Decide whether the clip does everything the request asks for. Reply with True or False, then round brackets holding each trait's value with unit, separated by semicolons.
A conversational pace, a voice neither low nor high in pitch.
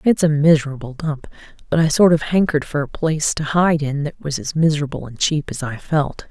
False (230 wpm; 150 Hz)